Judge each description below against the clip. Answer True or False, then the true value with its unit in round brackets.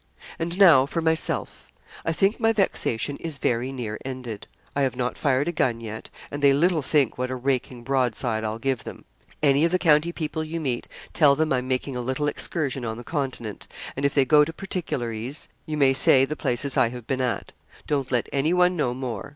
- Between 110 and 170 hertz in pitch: True (135 Hz)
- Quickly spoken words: True (210 wpm)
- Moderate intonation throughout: True (3.8 semitones)